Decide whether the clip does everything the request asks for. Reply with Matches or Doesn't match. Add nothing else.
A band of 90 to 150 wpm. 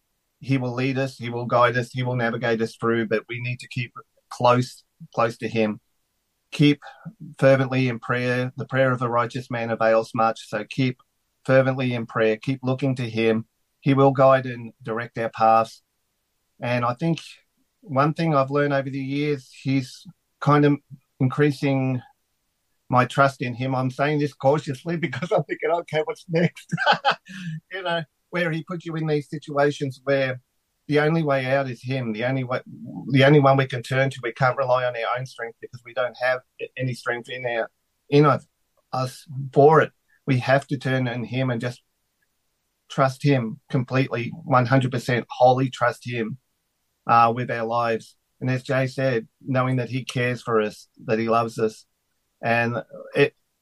Doesn't match